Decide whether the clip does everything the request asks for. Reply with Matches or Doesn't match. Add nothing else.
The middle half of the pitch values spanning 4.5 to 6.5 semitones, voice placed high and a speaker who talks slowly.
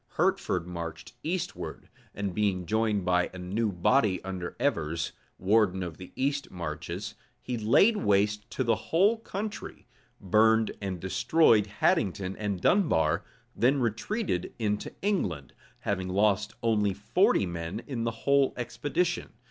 Doesn't match